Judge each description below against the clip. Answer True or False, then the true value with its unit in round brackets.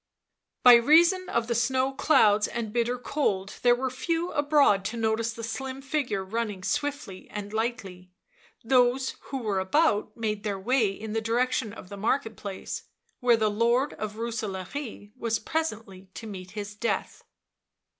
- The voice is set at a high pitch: True (230 Hz)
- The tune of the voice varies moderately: True (4.0 semitones)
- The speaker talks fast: False (165 wpm)